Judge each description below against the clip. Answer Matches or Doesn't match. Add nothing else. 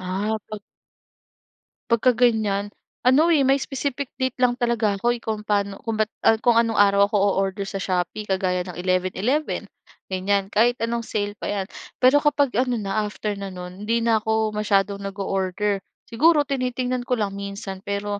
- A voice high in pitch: Matches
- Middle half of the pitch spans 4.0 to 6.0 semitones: Doesn't match